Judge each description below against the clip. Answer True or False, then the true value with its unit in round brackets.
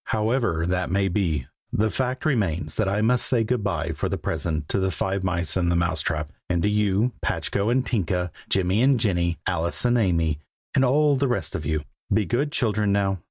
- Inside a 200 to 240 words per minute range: True (205 wpm)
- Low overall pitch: True (100 Hz)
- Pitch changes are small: False (5.0 semitones)